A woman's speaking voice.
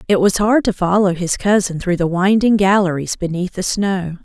Yes: female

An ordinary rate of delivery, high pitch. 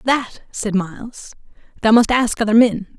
Yes: average, 160 wpm; high, 225 Hz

